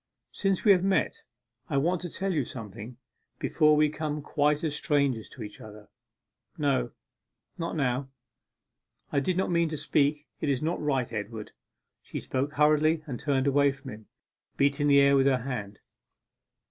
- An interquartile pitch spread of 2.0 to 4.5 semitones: Yes, average, 3.0 semitones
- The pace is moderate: Yes, average, 170 wpm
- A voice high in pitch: No, medium, 140 Hz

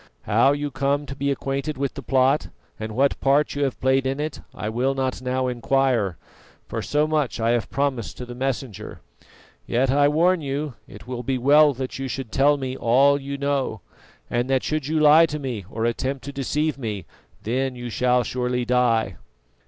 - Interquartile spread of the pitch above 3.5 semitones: No, narrow, 2.5 semitones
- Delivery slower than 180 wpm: No, average, 195 wpm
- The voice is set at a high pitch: No, low, 135 Hz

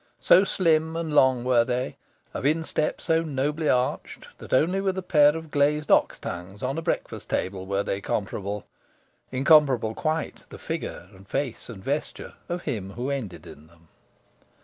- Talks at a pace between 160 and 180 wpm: Yes, average, 170 wpm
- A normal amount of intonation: No, wide, 7.4 semitones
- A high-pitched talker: No, low, 135 Hz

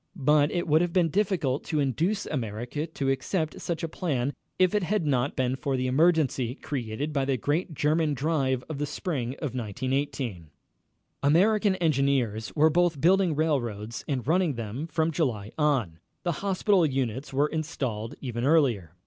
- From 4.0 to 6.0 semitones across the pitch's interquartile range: Yes, average, 4.4 semitones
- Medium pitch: Yes, medium, 145 Hz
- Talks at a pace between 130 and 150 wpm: No, average, 165 wpm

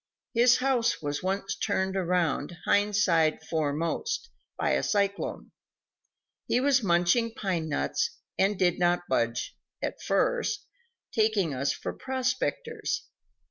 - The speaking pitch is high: Yes, high, 195 Hz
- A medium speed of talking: No, slow, 115 wpm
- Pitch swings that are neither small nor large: No, wide, 6.2 semitones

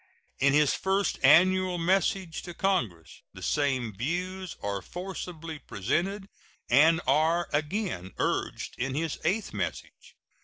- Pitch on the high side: No, medium, 165 Hz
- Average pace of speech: No, slow, 120 wpm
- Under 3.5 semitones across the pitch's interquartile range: No, wide, 5.4 semitones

